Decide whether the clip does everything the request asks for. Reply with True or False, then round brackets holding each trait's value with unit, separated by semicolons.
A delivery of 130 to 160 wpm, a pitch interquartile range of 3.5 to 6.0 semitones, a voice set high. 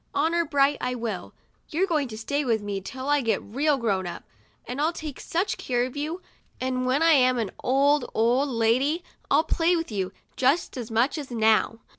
False (195 wpm; 4.5 semitones; 260 Hz)